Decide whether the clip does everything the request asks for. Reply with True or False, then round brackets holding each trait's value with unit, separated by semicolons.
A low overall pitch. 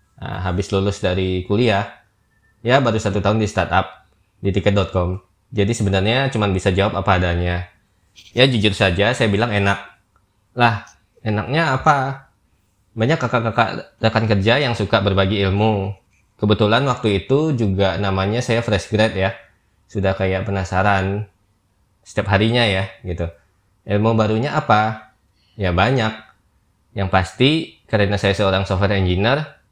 True (100 Hz)